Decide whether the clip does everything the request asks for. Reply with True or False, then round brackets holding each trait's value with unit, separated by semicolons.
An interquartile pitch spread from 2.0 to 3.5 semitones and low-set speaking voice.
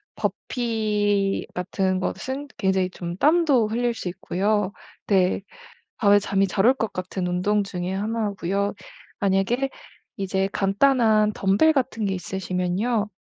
False (2.8 semitones; 200 Hz)